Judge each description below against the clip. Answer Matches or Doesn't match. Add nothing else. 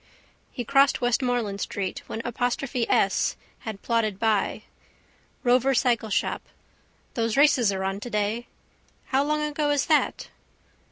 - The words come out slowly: Matches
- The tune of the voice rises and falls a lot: Doesn't match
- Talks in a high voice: Matches